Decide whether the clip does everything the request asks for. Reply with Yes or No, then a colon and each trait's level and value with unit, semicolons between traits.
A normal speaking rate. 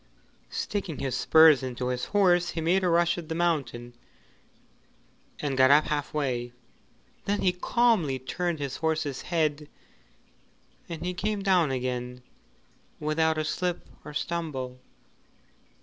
No: slow, 130 wpm